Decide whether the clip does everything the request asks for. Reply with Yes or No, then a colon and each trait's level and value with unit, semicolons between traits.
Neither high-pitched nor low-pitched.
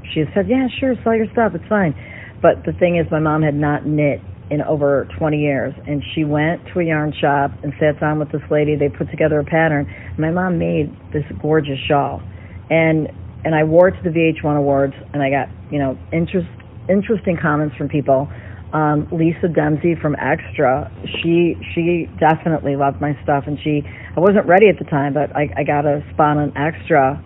Yes: medium, 150 Hz